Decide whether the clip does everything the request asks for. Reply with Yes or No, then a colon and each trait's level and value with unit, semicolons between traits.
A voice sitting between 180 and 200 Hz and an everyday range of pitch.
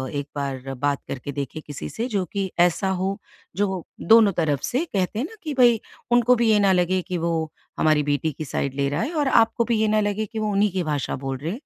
No: medium, 185 Hz; wide, 6.9 semitones